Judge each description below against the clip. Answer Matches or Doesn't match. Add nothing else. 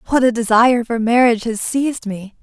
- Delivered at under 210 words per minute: Matches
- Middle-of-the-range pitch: Doesn't match